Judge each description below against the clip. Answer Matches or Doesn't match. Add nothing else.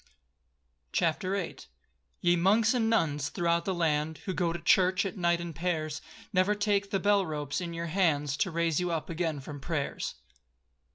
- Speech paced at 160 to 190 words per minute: Matches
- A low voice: Doesn't match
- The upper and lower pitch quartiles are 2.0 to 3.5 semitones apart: Matches